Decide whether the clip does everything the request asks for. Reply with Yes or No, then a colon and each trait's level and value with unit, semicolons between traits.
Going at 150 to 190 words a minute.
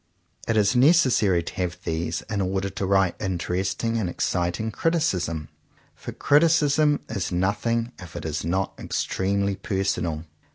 No: slow, 135 wpm